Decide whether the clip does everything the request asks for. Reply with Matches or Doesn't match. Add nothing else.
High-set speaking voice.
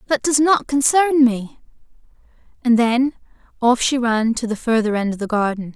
Matches